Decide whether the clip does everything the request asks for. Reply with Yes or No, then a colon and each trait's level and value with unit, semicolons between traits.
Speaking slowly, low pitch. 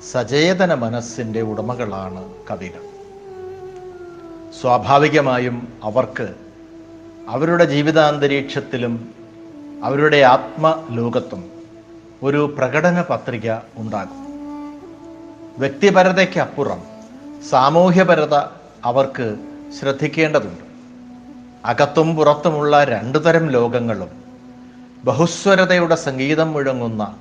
No: slow, 55 wpm; medium, 155 Hz